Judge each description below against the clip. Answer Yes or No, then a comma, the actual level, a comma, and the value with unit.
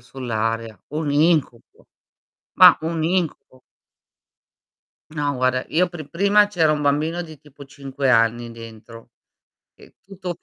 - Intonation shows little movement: No, wide, 5.4 semitones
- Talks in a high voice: No, medium, 145 Hz